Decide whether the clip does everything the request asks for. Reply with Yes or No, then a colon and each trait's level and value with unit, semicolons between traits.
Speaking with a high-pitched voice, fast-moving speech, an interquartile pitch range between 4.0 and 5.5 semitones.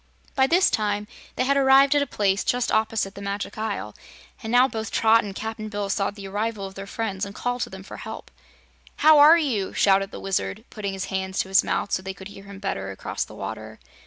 No: high, 205 Hz; fast, 230 wpm; average, 2.8 semitones